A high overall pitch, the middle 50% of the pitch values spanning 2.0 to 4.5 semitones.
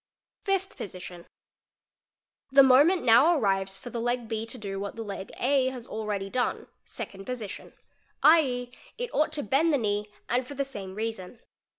No: high, 240 Hz; average, 5.1 semitones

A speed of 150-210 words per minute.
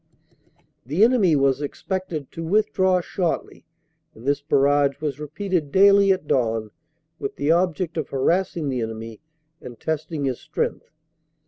No: average, 140 wpm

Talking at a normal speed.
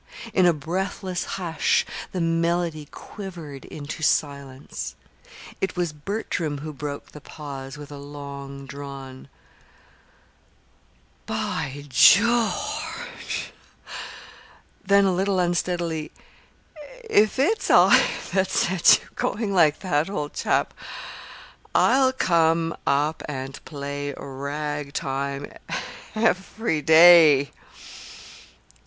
No: slow, 95 wpm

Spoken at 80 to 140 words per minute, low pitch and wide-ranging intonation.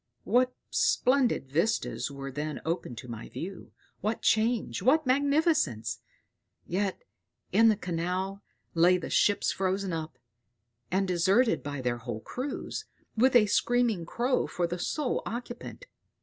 No: slow, 135 wpm; high, 190 Hz; wide, 7.0 semitones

